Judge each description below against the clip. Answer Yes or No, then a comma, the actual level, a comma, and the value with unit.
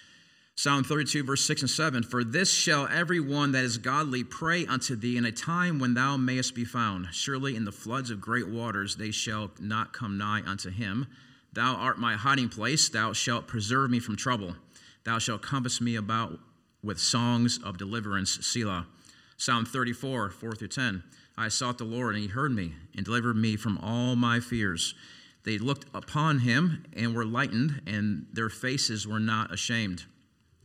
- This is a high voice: No, low, 120 Hz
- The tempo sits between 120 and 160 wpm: No, average, 180 wpm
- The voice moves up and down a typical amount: Yes, average, 3.5 semitones